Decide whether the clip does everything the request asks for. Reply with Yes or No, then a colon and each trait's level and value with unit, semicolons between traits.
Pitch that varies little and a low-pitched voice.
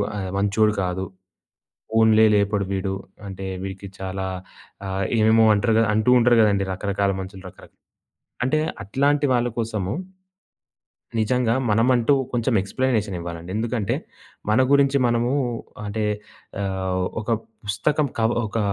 No: average, 3.3 semitones; low, 105 Hz